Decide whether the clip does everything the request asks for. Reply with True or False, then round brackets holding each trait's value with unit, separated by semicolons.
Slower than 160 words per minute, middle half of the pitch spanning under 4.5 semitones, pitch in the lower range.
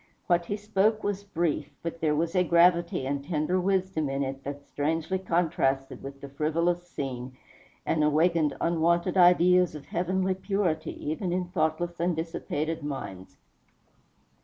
False (145 wpm; 3.3 semitones; 170 Hz)